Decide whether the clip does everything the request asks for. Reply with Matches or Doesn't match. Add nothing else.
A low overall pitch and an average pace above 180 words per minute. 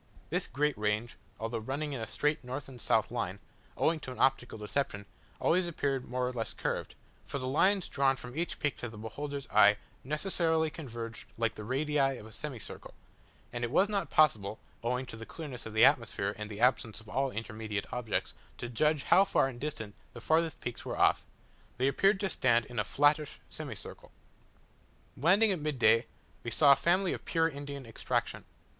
Matches